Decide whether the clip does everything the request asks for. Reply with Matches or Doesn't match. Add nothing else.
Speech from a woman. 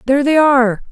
Matches